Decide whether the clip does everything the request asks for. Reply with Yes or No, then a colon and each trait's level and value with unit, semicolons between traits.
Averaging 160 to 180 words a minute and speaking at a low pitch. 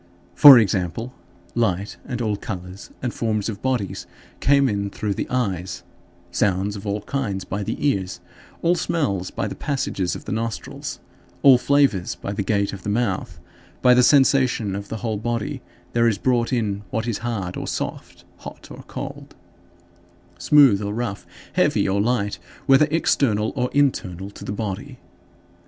Yes: average, 165 wpm; low, 110 Hz